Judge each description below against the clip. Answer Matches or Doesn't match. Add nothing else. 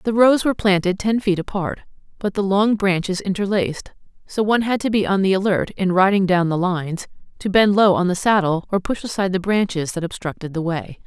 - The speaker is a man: Doesn't match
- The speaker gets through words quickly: Matches